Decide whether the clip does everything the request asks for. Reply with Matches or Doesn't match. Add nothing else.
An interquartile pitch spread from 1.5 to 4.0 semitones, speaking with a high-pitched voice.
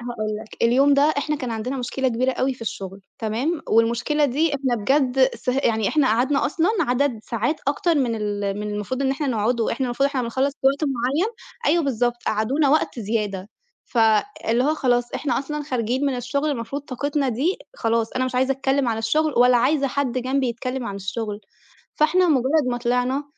Matches